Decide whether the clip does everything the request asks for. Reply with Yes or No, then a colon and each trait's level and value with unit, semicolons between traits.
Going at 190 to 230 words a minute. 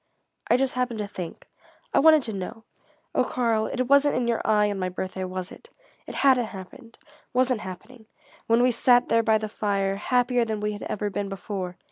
Yes: average, 200 wpm